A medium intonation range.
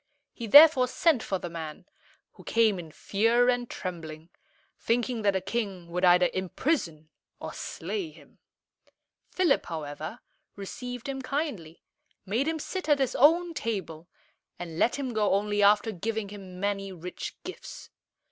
No: wide, 5.9 semitones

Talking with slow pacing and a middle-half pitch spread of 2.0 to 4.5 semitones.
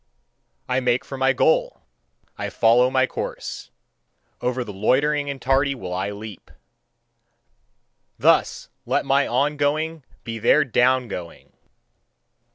Yes: slow, 125 wpm; average, 3.4 semitones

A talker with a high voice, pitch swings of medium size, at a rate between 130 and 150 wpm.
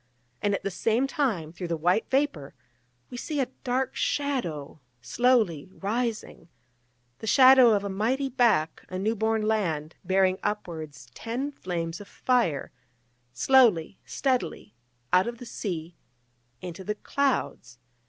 No: high, 210 Hz; wide, 6.7 semitones; slow, 135 wpm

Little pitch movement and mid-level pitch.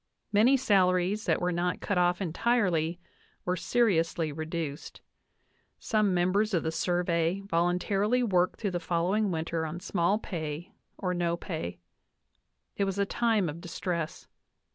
No: average, 3.1 semitones; medium, 180 Hz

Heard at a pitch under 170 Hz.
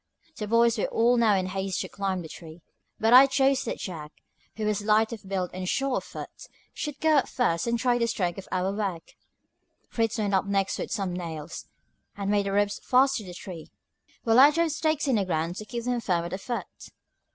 No: high, 205 Hz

